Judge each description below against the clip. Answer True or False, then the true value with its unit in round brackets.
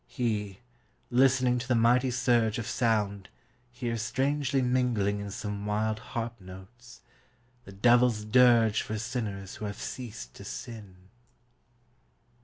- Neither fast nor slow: False (125 wpm)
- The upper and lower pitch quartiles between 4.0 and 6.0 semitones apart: False (3.2 semitones)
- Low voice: True (115 Hz)